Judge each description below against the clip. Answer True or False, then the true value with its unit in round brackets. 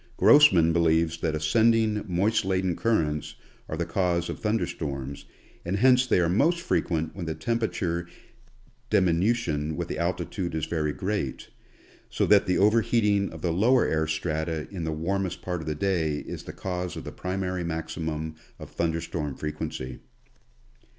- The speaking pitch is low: True (85 Hz)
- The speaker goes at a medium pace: True (160 wpm)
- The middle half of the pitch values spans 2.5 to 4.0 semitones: True (3.7 semitones)